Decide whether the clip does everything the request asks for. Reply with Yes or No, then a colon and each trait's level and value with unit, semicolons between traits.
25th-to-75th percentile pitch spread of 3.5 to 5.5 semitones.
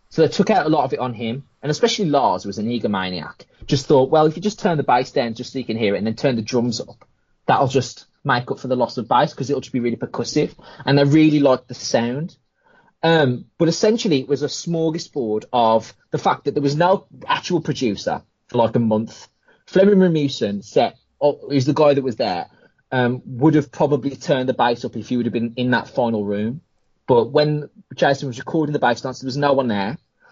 Yes: average, 4.0 semitones